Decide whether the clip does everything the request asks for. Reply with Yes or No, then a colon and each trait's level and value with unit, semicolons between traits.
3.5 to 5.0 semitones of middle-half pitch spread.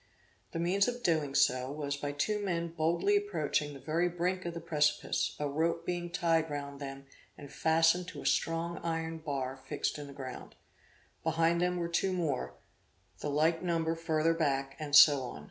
No: average, 2.9 semitones